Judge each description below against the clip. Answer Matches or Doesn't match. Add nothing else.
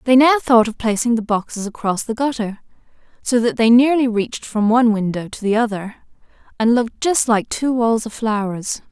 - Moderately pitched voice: Doesn't match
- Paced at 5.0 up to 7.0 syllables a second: Matches